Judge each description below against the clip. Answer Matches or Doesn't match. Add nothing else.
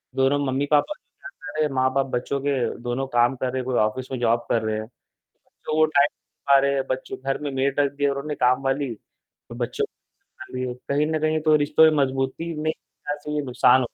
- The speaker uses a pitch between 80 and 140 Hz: Matches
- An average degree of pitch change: Doesn't match